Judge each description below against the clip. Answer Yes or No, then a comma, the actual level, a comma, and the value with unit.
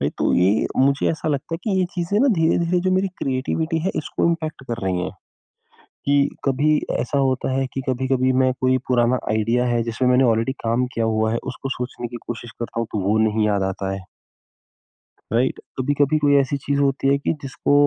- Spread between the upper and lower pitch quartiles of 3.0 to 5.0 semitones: Yes, average, 3.6 semitones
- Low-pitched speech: Yes, low, 130 Hz